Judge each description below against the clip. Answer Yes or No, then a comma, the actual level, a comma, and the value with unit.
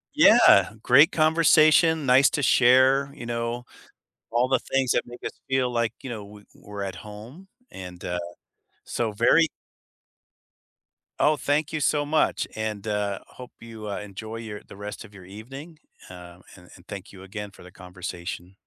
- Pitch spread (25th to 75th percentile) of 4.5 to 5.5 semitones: Yes, average, 5.0 semitones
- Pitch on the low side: Yes, low, 115 Hz